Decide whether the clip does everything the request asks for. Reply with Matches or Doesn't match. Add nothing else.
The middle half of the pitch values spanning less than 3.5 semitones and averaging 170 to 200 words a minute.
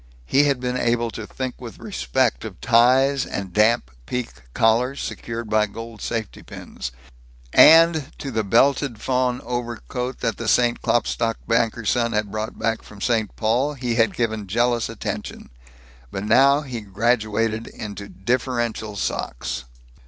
Doesn't match